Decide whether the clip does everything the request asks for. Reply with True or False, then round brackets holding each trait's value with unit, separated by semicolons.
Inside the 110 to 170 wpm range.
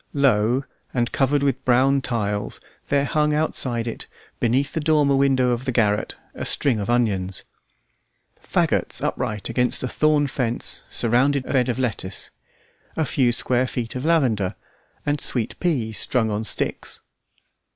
True (150 wpm)